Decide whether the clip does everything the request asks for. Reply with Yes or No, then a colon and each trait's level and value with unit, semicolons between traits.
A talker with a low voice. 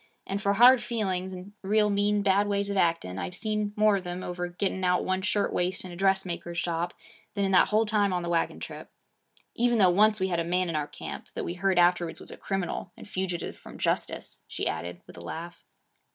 No: high, 190 Hz